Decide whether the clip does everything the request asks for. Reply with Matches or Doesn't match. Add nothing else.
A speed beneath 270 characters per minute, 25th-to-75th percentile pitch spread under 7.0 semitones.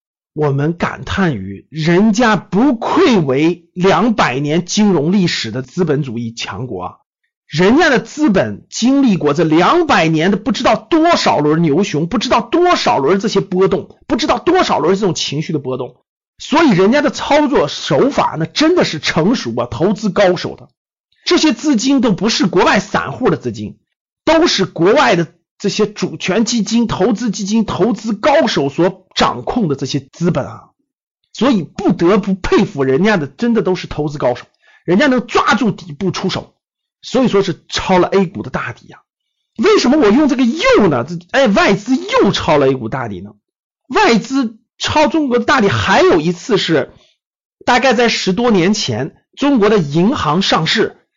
Doesn't match